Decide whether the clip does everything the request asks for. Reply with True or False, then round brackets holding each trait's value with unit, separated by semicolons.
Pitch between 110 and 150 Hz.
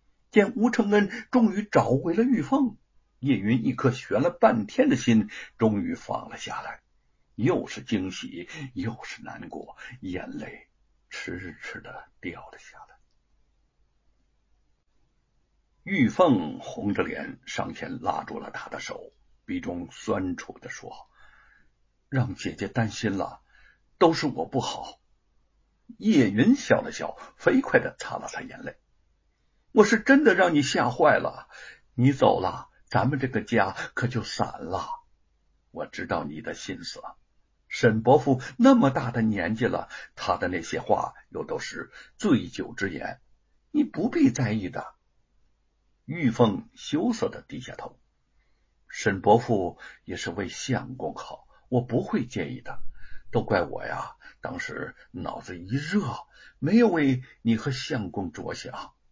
True (140 Hz)